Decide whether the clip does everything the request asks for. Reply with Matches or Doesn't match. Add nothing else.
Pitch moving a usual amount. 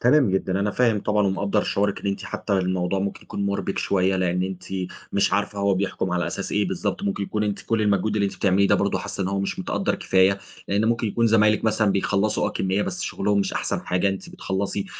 Doesn't match